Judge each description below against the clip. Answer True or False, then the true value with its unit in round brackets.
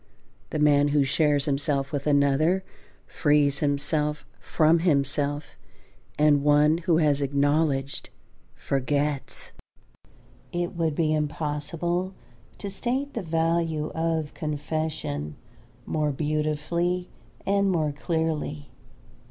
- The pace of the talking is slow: True (100 wpm)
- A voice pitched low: False (150 Hz)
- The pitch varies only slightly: True (2.2 semitones)